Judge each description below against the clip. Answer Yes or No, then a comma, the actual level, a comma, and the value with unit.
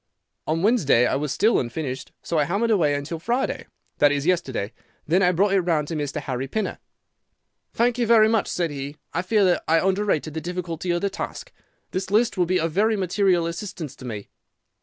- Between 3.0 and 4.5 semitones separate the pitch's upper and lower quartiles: No, average, 5.2 semitones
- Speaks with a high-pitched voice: No, medium, 175 Hz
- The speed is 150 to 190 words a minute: No, average, 200 wpm